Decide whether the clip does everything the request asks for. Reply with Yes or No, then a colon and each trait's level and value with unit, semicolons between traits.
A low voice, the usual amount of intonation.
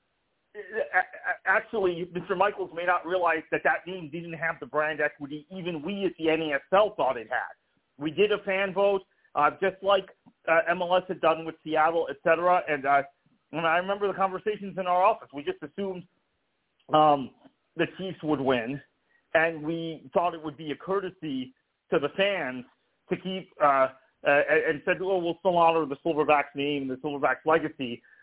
No: medium, 165 Hz; average, 3.9 semitones